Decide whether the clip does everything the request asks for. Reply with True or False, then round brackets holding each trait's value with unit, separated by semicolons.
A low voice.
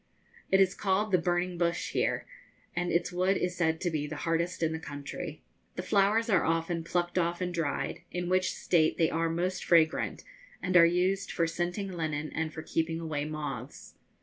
False (170 Hz)